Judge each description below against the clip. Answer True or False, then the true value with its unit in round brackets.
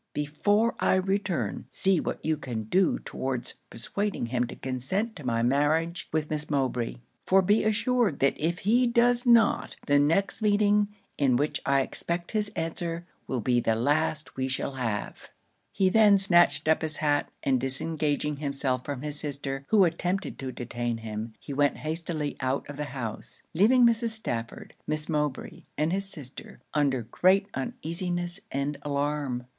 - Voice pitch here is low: False (150 Hz)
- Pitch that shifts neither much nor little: False (6.0 semitones)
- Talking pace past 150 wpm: True (160 wpm)